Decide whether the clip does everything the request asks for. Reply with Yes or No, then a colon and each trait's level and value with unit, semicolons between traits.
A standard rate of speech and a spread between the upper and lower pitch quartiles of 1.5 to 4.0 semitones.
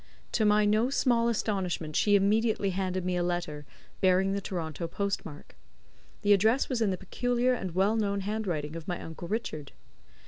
Yes: average, 175 wpm; average, 3.7 semitones